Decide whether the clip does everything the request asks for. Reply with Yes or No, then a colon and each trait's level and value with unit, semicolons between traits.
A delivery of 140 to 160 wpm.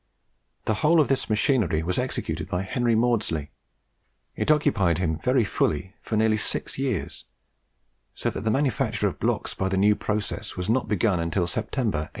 No: average, 170 wpm